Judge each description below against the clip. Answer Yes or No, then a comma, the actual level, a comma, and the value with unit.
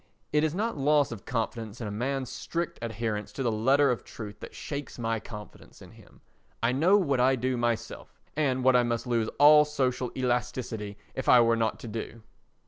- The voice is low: Yes, low, 125 Hz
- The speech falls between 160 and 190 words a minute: No, average, 200 wpm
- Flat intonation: No, average, 3.5 semitones